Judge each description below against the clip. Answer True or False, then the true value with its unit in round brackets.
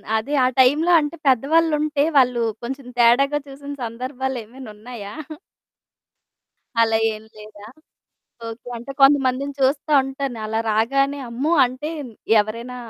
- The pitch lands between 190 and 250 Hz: False (260 Hz)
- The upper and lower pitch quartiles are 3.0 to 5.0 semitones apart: True (3.5 semitones)